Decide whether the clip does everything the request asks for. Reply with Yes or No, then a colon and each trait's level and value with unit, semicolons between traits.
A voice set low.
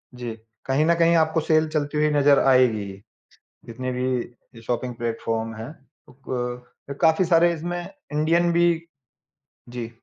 No: medium, 145 Hz